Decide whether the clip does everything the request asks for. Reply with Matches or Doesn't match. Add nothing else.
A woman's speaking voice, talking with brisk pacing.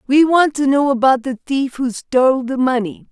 Matches